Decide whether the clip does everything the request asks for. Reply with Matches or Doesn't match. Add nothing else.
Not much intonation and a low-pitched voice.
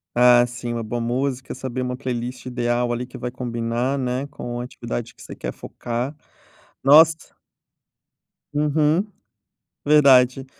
Matches